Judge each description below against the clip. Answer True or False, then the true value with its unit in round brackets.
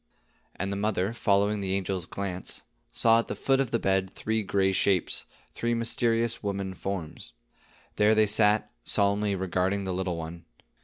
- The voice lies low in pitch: True (100 Hz)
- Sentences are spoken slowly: False (160 wpm)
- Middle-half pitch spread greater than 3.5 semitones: False (2.4 semitones)